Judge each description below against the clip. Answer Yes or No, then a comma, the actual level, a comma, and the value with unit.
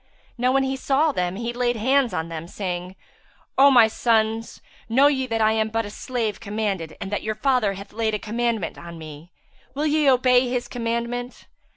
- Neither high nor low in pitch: No, high, 230 Hz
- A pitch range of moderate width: Yes, average, 3.6 semitones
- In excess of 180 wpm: Yes, average, 190 wpm